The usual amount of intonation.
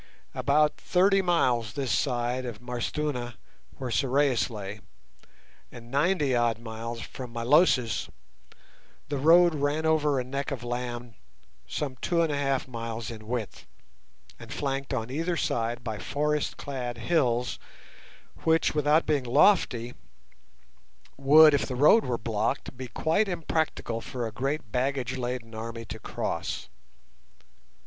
Yes: average, 4.0 semitones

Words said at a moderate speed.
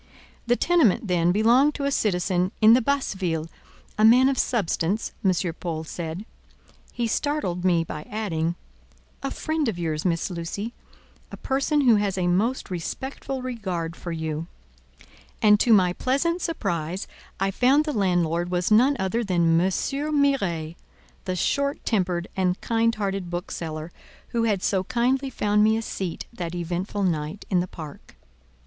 Yes: average, 155 wpm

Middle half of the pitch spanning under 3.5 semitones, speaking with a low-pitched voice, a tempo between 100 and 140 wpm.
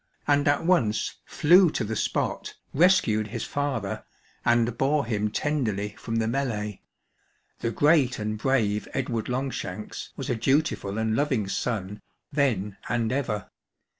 No: average, 4.7 semitones; low, 115 Hz; slow, 135 wpm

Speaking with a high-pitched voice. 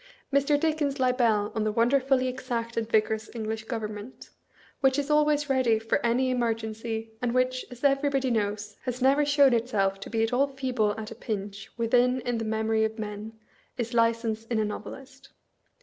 Yes: high, 235 Hz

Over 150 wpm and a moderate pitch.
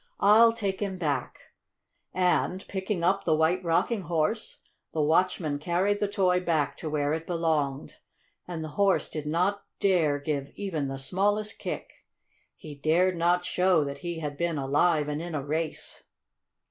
Yes: average, 160 wpm; medium, 170 Hz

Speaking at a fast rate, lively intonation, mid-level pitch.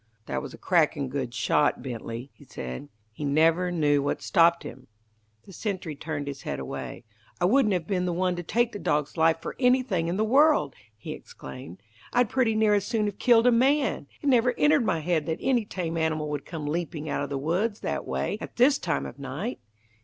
Yes: fast, 215 wpm; wide, 7.1 semitones; medium, 170 Hz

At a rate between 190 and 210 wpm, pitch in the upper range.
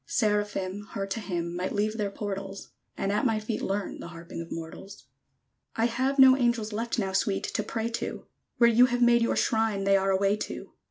Yes: fast, 205 wpm; high, 210 Hz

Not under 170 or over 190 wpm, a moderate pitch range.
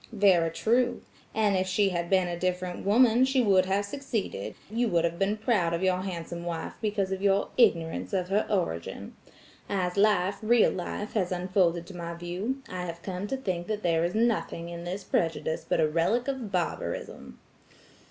Yes: average, 185 wpm; average, 3.6 semitones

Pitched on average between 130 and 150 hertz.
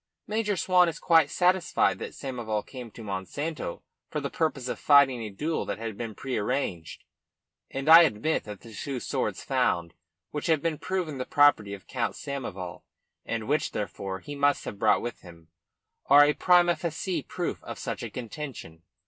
Yes: low, 135 Hz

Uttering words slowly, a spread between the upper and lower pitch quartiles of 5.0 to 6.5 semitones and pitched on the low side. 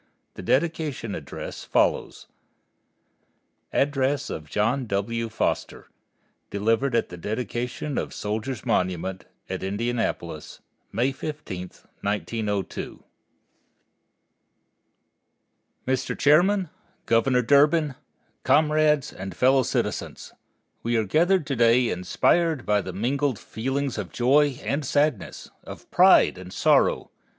Yes: slow, 100 wpm; wide, 5.4 semitones; low, 125 Hz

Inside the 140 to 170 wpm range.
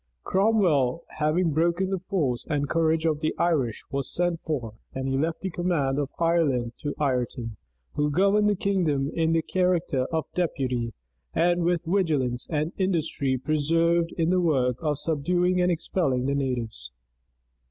Yes: average, 155 wpm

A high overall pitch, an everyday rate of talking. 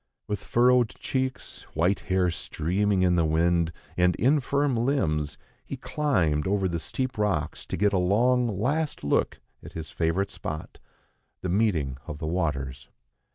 No: very low, 95 Hz; average, 150 wpm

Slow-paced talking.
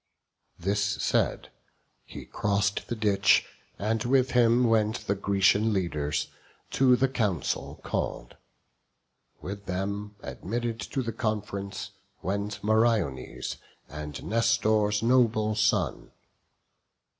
Yes: slow, 100 wpm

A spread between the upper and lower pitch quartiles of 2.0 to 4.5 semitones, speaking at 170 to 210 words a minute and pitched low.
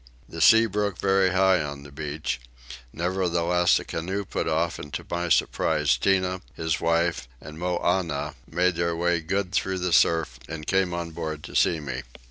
Yes: average, 2.8 semitones; average, 175 wpm; very low, 85 Hz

